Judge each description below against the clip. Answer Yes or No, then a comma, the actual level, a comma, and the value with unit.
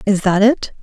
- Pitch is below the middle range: No, high, 205 Hz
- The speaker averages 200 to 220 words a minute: Yes, fast, 215 wpm